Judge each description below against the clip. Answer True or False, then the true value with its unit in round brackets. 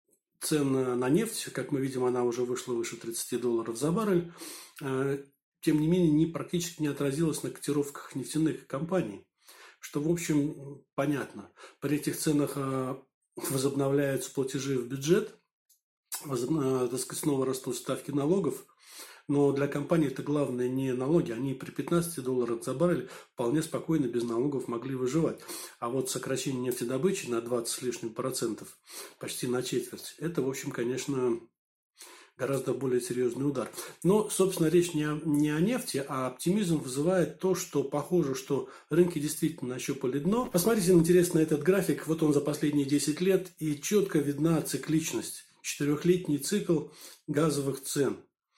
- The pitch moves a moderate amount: True (3.8 semitones)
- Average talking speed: False (145 wpm)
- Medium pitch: True (145 Hz)